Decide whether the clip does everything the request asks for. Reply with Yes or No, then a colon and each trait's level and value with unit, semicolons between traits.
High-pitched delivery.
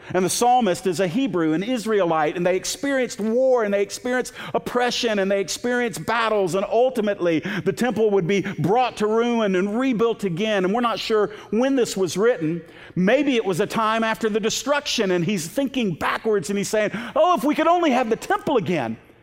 Yes: high, 220 Hz